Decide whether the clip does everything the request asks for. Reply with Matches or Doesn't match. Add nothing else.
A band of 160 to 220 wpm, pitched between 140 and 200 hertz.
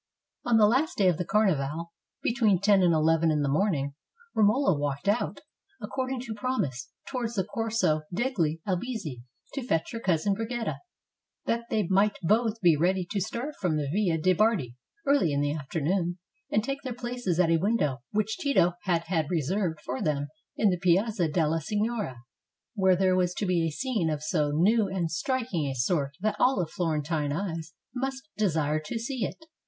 Matches